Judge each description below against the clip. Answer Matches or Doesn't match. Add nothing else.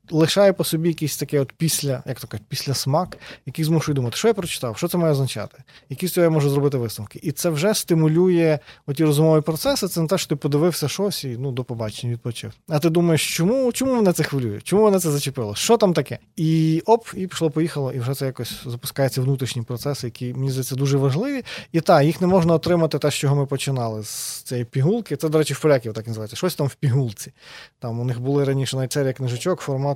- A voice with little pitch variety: Doesn't match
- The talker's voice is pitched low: Doesn't match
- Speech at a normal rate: Doesn't match